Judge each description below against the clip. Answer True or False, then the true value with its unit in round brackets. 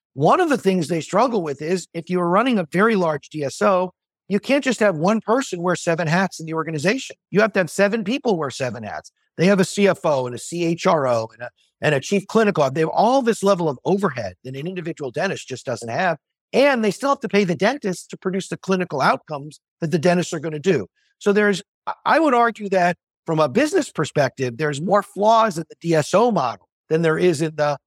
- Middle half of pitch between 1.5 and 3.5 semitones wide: False (4.4 semitones)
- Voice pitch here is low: False (180 Hz)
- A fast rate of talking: True (225 wpm)